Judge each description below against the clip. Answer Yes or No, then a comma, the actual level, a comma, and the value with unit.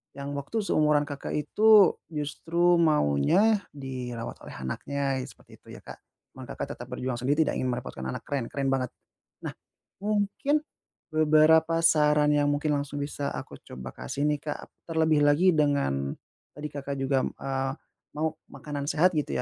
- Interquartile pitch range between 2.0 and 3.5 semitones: Yes, average, 2.9 semitones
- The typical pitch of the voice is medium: Yes, medium, 145 Hz